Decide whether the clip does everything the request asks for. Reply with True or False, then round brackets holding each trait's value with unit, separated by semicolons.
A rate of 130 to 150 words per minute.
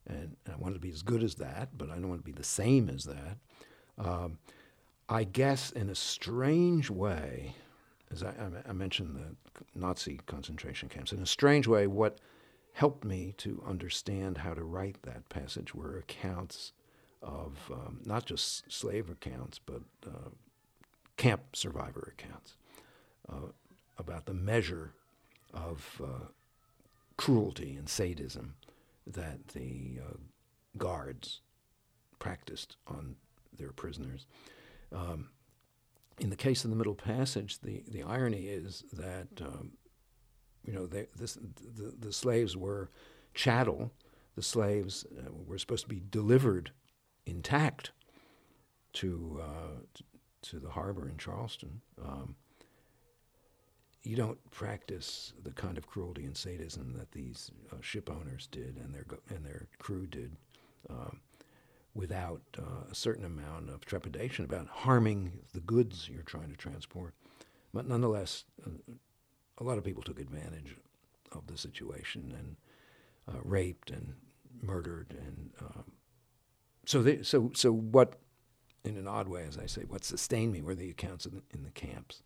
True (145 wpm)